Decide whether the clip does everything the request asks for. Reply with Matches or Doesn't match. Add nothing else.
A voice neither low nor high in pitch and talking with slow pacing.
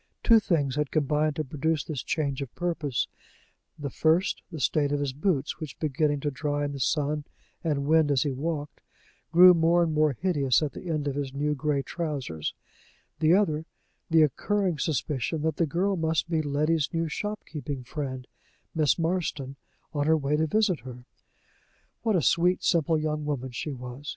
Doesn't match